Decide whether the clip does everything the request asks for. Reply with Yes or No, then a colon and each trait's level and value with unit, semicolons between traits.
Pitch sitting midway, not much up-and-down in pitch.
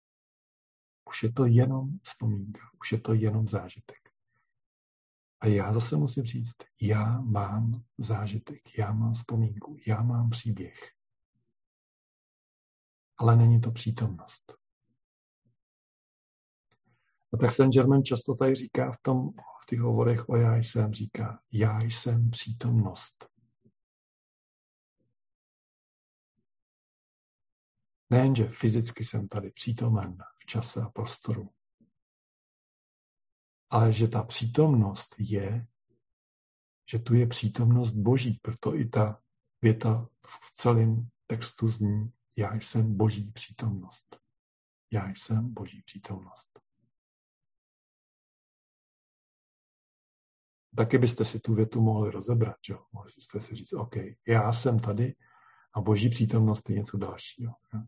No: low, 115 Hz; narrow, 1.9 semitones